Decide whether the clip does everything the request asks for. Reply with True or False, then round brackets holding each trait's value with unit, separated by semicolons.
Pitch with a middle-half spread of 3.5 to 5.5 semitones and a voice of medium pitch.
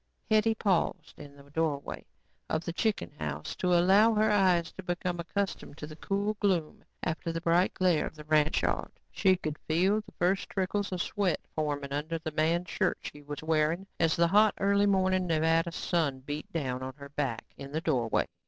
True (3.9 semitones; 165 Hz)